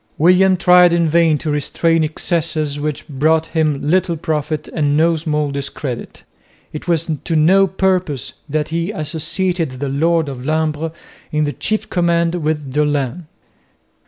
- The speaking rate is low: No, average, 145 wpm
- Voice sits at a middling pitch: Yes, medium, 160 Hz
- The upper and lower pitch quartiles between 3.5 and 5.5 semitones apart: No, narrow, 2.4 semitones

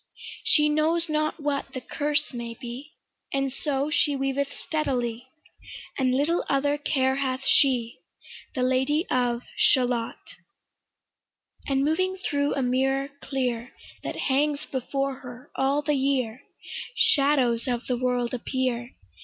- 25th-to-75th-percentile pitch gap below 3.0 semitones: Yes, narrow, 2.6 semitones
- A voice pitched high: Yes, very high, 270 Hz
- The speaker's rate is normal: No, slow, 130 wpm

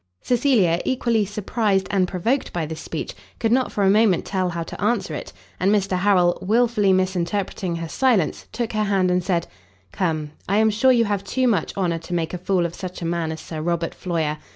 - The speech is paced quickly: Yes, fast, 210 wpm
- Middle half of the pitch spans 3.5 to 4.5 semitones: Yes, average, 3.9 semitones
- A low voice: No, high, 190 Hz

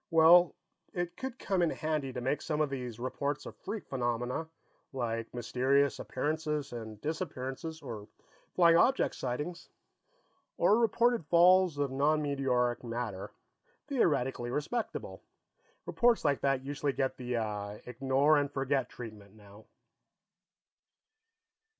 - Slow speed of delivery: Yes, slow, 120 wpm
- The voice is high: No, medium, 140 Hz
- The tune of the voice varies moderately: Yes, average, 4.7 semitones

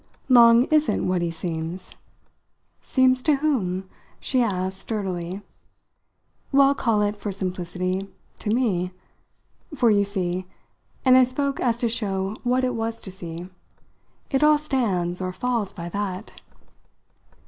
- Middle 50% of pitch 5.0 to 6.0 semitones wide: Yes, wide, 5.5 semitones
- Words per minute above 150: No, slow, 135 wpm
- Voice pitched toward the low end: No, high, 205 Hz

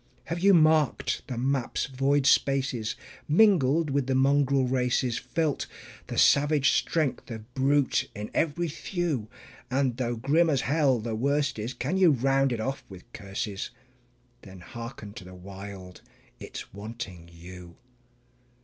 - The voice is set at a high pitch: No, low, 130 Hz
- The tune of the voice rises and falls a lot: No, average, 4.7 semitones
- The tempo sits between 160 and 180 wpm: No, average, 140 wpm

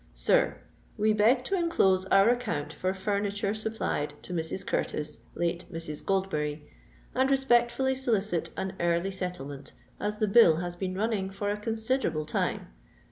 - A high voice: Yes, high, 195 Hz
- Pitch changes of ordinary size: Yes, average, 4.4 semitones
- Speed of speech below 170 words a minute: Yes, average, 150 wpm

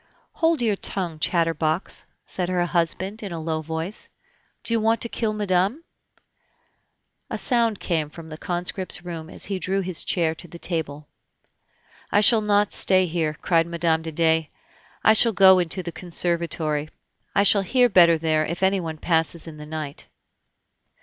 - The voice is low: No, medium, 175 Hz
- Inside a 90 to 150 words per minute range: No, average, 165 wpm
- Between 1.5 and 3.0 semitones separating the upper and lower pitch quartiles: No, average, 3.4 semitones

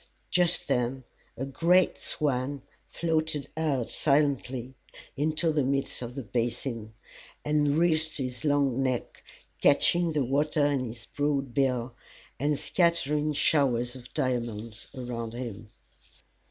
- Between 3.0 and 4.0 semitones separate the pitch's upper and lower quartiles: Yes, average, 3.6 semitones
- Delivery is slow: Yes, slow, 120 wpm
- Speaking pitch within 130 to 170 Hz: Yes, low, 135 Hz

